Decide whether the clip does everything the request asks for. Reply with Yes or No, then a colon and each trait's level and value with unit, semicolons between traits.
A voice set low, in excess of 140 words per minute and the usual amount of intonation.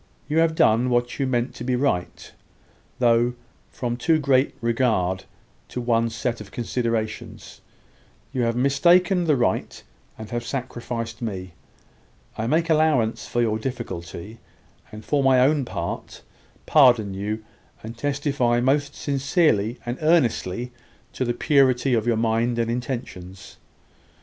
No: low, 120 Hz; slow, 135 wpm; average, 3.2 semitones